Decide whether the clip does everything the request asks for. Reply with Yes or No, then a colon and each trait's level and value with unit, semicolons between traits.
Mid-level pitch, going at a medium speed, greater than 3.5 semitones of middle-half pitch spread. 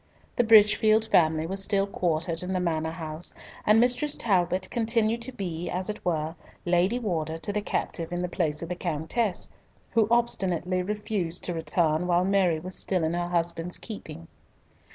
Yes: medium, 180 Hz; average, 175 wpm; average, 4.1 semitones